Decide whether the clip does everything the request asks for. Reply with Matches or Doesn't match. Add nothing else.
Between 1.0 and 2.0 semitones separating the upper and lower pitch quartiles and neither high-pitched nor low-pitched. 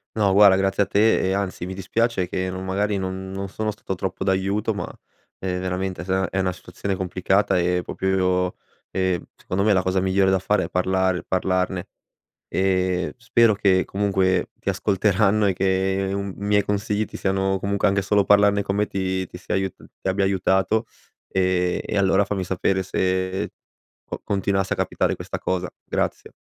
Doesn't match